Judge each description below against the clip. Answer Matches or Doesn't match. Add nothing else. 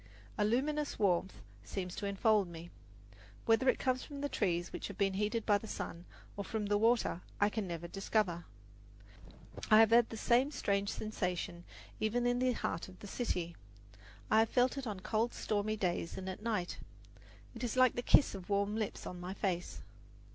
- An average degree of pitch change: Matches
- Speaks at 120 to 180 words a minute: Doesn't match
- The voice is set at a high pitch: Matches